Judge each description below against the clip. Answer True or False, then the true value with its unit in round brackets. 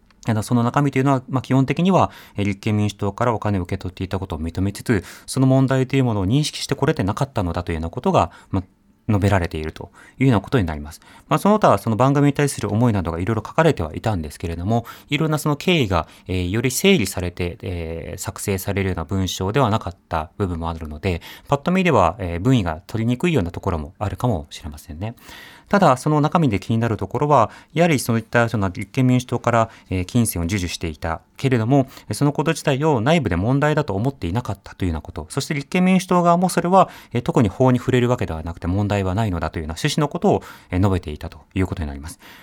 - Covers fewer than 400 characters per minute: False (470 characters per minute)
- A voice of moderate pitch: False (110 Hz)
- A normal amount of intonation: False (6.9 semitones)